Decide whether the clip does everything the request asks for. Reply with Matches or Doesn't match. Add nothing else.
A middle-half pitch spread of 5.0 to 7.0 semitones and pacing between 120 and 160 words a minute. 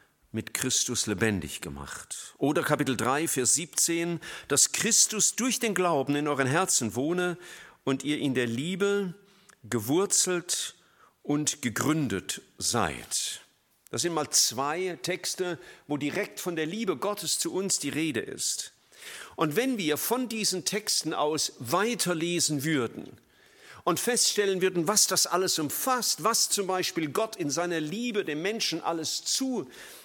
Matches